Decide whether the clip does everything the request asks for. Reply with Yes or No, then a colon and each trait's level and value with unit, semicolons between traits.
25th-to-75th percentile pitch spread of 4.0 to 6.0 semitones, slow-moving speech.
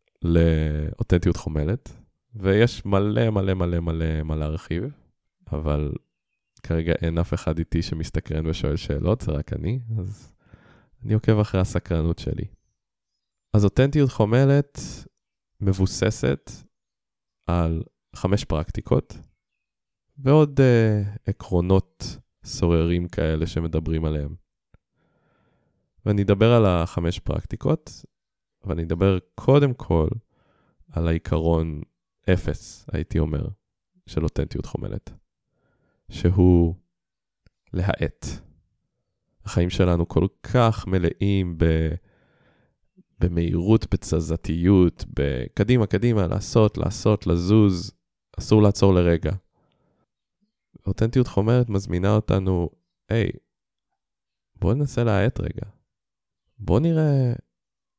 Yes: average, 4.7 semitones; slow, 90 wpm